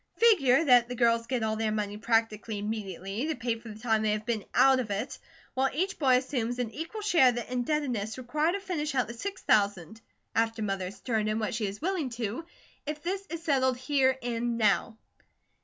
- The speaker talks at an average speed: No, fast, 210 wpm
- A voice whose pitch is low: No, high, 240 Hz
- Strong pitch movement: No, average, 4.2 semitones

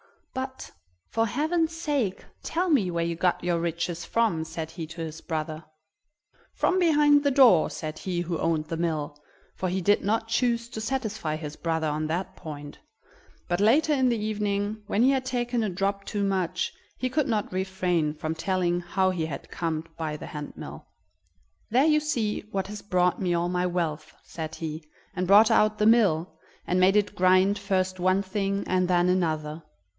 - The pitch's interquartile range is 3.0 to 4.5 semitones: No, average, 4.9 semitones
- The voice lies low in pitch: No, medium, 185 Hz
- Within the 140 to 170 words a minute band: No, average, 185 wpm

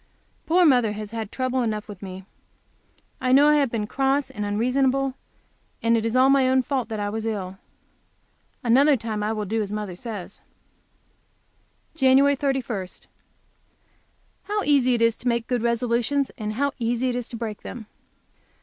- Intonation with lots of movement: No, average, 3.7 semitones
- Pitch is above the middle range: Yes, high, 235 Hz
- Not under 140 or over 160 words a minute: No, average, 170 wpm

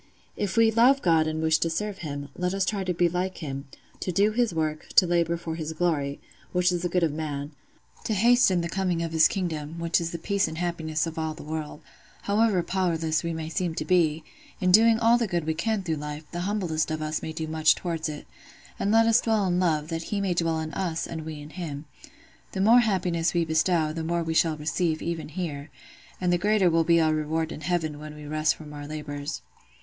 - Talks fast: Yes, fast, 230 wpm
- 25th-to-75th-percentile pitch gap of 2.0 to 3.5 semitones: Yes, average, 2.8 semitones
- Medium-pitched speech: Yes, medium, 165 Hz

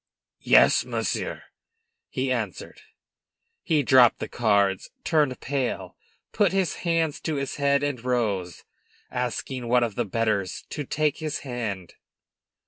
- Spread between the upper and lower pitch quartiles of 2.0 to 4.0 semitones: No, average, 4.5 semitones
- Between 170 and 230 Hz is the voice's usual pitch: No, low, 125 Hz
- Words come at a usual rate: No, slow, 130 wpm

